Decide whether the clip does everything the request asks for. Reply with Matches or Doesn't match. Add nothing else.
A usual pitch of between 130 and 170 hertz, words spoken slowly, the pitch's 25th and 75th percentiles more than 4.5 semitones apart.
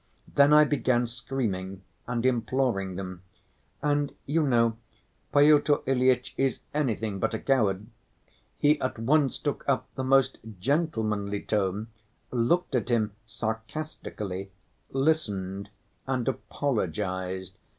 Doesn't match